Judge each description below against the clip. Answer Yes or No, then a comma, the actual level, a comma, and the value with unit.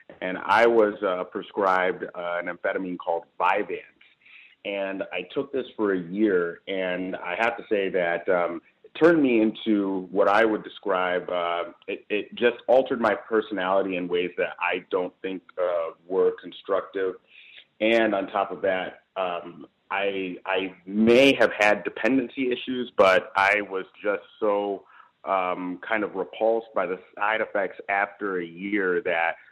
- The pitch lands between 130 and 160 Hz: No, very low, 95 Hz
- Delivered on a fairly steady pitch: No, average, 3.1 semitones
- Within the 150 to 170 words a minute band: Yes, average, 160 wpm